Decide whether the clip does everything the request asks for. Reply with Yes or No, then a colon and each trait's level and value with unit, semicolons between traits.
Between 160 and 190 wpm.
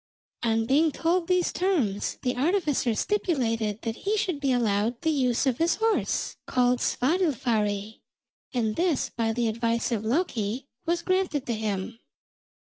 No: average, 145 wpm